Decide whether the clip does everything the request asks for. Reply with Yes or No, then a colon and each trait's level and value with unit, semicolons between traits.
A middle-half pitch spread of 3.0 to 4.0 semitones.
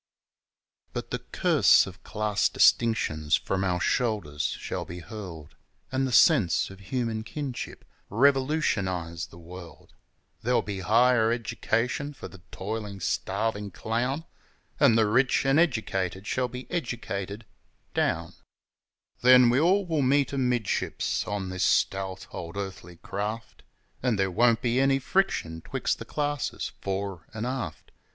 No: average, 5.0 semitones